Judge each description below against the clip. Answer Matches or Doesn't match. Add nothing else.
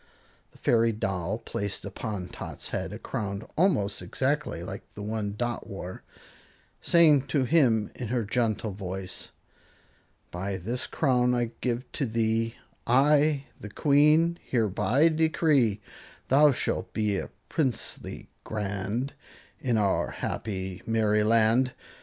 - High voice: Doesn't match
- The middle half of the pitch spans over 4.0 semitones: Matches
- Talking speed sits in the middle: Doesn't match